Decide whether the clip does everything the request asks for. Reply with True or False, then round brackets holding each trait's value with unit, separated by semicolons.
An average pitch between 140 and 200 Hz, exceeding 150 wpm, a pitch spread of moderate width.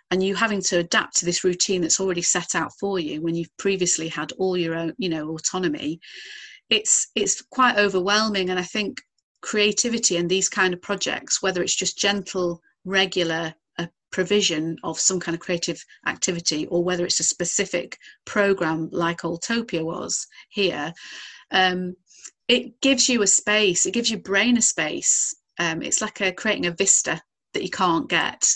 True (185 Hz; 175 wpm; 3.0 semitones)